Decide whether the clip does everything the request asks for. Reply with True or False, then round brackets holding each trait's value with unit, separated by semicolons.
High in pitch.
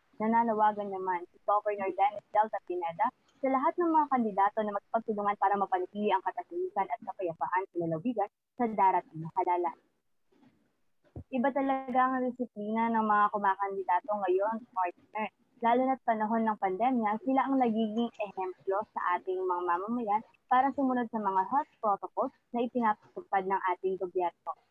True (210 Hz)